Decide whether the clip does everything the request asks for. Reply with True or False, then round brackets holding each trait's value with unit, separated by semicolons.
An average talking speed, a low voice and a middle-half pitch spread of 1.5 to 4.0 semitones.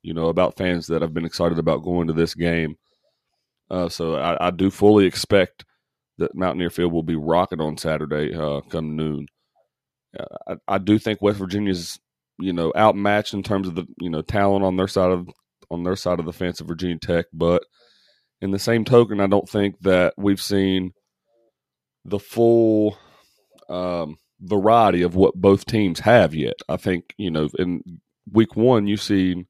True (185 wpm; 90 Hz; 2.9 semitones)